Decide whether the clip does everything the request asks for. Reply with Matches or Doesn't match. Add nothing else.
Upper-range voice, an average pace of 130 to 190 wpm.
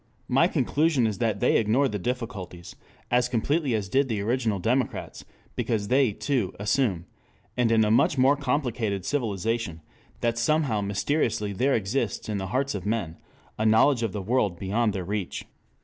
Doesn't match